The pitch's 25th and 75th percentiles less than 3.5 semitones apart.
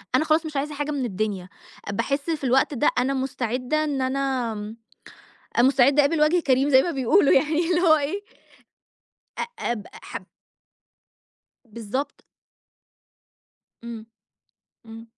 No: average, 4.0 semitones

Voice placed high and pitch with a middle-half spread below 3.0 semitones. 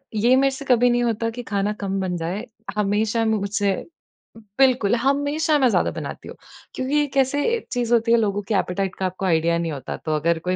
No: high, 220 Hz; average, 4.6 semitones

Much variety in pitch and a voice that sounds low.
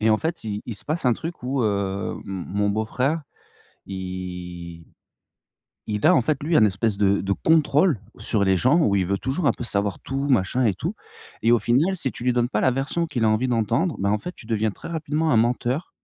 Yes: wide, 5.8 semitones; low, 115 Hz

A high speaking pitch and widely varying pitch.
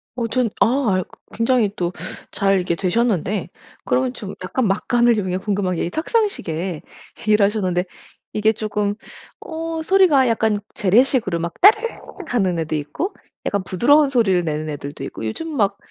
Yes: high, 210 Hz; wide, 5.7 semitones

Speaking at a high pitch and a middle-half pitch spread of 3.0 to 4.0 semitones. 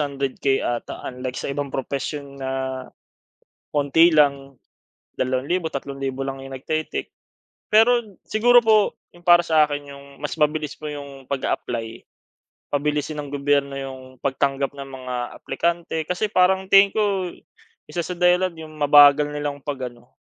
No: medium, 145 Hz; average, 3.6 semitones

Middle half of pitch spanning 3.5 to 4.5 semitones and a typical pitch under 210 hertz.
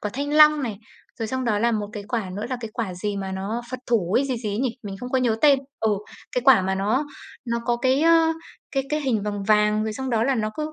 No: average, 4.1 semitones; high, 230 Hz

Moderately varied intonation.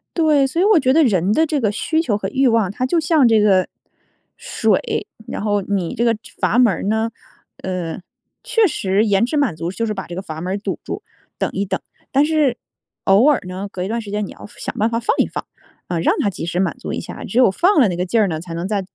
No: wide, 5.9 semitones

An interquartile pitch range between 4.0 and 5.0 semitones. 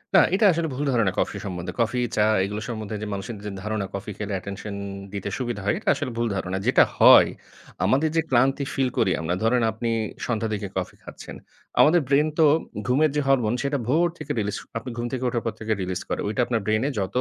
Yes: average, 4.5 semitones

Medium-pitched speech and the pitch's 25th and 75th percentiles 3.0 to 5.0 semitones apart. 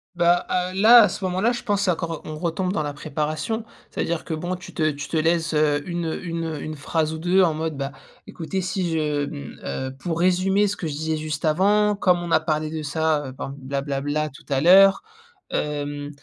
Yes: medium, 160 Hz; average, 3.3 semitones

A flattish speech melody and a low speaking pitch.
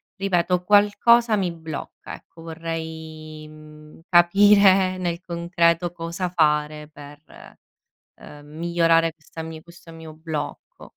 No: narrow, 2.3 semitones; medium, 165 Hz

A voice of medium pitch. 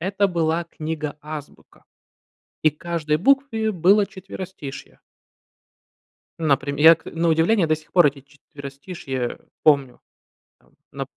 Yes: medium, 160 Hz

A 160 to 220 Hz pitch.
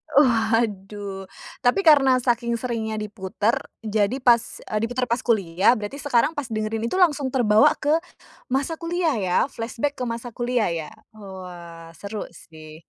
No: high, 230 Hz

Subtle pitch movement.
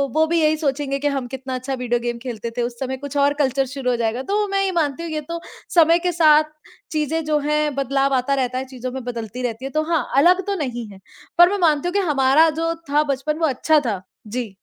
No: average, 3.8 semitones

